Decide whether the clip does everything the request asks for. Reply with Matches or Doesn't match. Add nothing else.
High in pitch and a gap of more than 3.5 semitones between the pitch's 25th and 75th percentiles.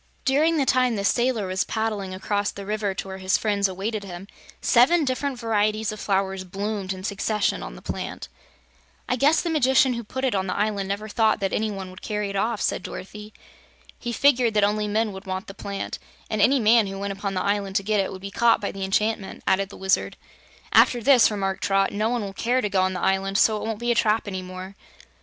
Doesn't match